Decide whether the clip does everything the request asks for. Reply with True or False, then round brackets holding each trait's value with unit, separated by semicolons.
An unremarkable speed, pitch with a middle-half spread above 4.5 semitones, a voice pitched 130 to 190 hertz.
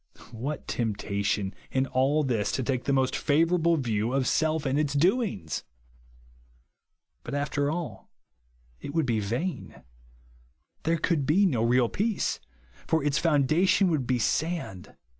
True (145 wpm; 4.9 semitones; 140 Hz)